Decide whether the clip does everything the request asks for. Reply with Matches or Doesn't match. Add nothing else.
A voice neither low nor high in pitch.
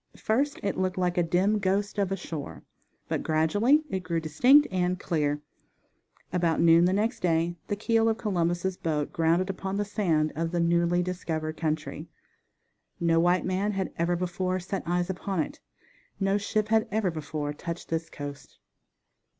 Matches